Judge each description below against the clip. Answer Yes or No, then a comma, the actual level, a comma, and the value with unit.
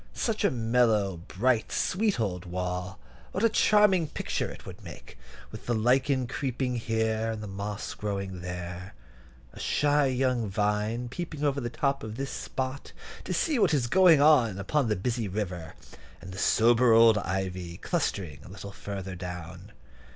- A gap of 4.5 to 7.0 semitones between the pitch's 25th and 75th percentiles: Yes, wide, 5.6 semitones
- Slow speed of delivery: No, average, 165 wpm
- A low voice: Yes, low, 110 Hz